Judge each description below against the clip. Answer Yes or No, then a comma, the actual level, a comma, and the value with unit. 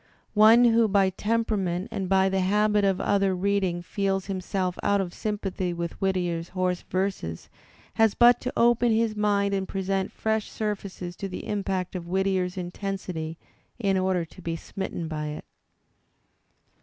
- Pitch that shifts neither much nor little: No, narrow, 2.2 semitones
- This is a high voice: Yes, high, 195 Hz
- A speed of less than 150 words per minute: No, average, 155 wpm